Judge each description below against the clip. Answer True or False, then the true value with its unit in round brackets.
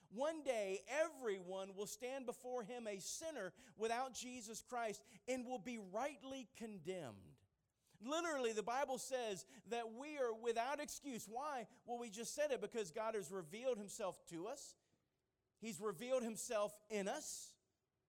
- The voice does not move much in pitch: False (3.8 semitones)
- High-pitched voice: True (230 Hz)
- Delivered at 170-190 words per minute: False (145 wpm)